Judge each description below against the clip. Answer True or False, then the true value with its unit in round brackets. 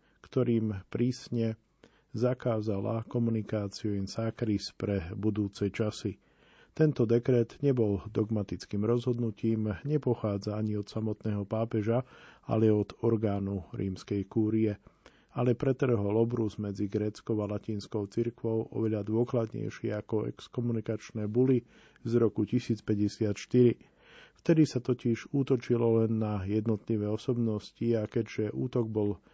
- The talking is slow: True (105 wpm)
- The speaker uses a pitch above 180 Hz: False (110 Hz)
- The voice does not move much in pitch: True (2.2 semitones)